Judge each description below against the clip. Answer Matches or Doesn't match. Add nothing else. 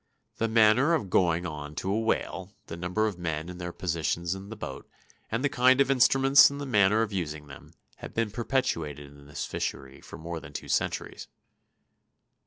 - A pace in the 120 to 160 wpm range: Doesn't match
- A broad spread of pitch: Matches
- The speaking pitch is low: Matches